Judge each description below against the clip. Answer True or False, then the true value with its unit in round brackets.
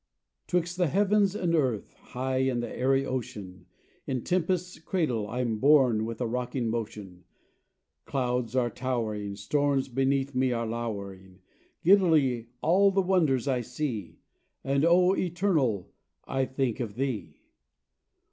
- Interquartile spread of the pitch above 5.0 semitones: True (5.6 semitones)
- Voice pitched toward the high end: False (130 Hz)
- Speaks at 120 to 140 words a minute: True (135 wpm)